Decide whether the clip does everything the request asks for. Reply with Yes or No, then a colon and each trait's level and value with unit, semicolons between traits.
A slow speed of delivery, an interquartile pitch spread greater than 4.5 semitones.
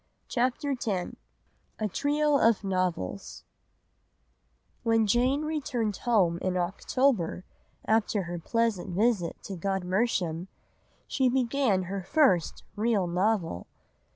Yes: slow, 100 wpm; average, 5.1 semitones